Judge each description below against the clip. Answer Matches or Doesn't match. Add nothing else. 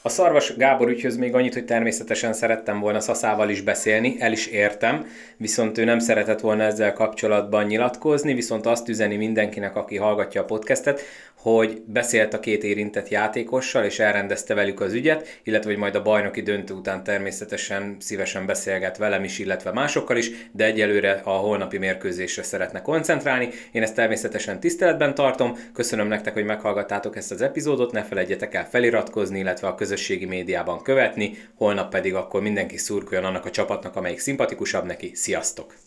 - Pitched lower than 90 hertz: Doesn't match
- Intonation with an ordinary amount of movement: Doesn't match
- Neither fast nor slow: Doesn't match